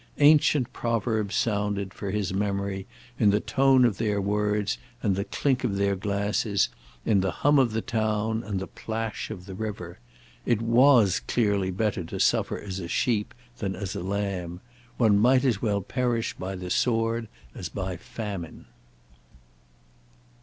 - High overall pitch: No, low, 105 Hz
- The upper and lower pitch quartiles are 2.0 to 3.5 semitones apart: Yes, average, 2.8 semitones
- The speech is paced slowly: No, average, 160 wpm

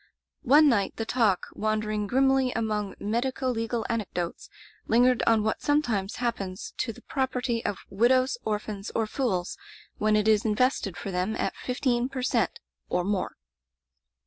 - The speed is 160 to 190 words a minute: No, average, 145 wpm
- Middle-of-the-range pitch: No, high, 225 Hz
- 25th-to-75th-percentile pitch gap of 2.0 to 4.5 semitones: Yes, average, 3.4 semitones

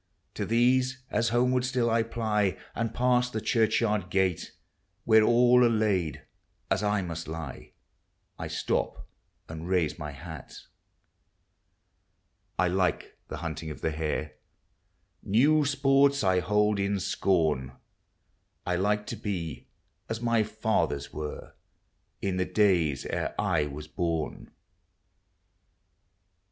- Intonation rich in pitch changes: Yes, wide, 5.8 semitones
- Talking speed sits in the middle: No, slow, 120 wpm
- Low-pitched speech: Yes, low, 100 Hz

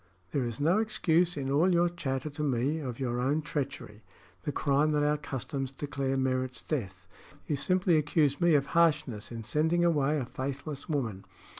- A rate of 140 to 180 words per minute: Yes, average, 175 wpm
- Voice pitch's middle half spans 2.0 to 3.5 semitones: Yes, average, 3.2 semitones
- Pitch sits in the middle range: Yes, medium, 145 Hz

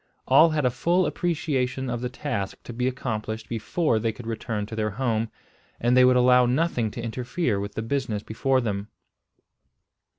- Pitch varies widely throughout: No, average, 3.0 semitones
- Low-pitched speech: Yes, low, 125 Hz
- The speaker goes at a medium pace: Yes, average, 175 wpm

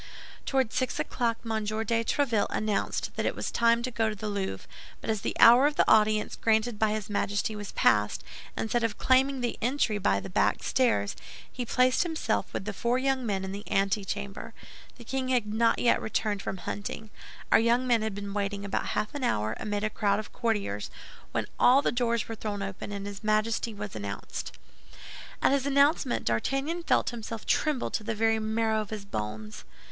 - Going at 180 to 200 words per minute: Yes, average, 195 wpm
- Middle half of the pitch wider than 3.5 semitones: No, average, 2.9 semitones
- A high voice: Yes, high, 220 Hz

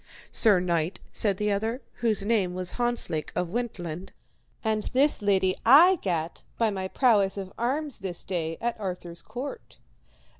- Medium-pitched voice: No, high, 200 Hz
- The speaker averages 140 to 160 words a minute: Yes, average, 150 wpm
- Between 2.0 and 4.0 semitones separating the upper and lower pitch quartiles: No, average, 4.7 semitones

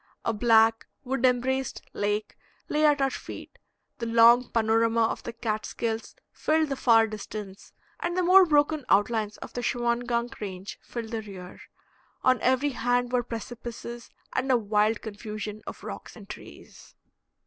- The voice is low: No, high, 235 Hz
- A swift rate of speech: No, average, 150 wpm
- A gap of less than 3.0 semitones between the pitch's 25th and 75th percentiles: Yes, narrow, 2.5 semitones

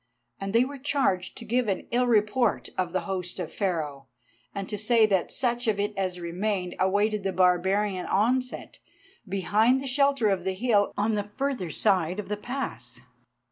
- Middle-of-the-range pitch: No, high, 205 Hz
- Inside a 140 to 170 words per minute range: No, average, 180 wpm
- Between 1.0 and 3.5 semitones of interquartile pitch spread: No, average, 4.1 semitones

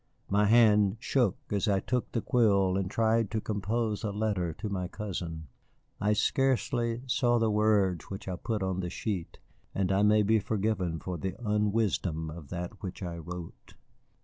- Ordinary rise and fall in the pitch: Yes, average, 3.2 semitones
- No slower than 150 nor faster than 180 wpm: Yes, average, 175 wpm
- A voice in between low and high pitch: No, low, 105 Hz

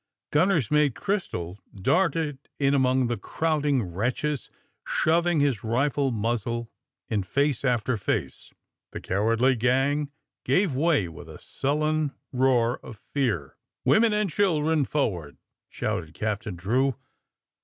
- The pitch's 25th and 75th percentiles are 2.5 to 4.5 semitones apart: No, average, 4.9 semitones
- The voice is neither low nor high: No, low, 130 Hz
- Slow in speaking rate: Yes, slow, 120 wpm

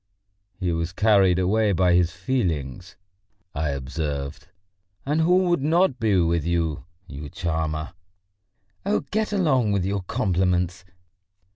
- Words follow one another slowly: Yes, slow, 125 wpm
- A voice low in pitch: Yes, very low, 90 Hz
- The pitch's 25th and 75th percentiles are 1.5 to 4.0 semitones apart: No, average, 5.2 semitones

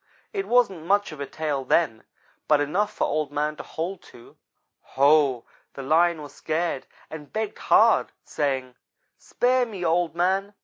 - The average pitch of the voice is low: No, medium, 160 Hz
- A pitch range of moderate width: Yes, average, 4.9 semitones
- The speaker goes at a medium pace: Yes, average, 160 wpm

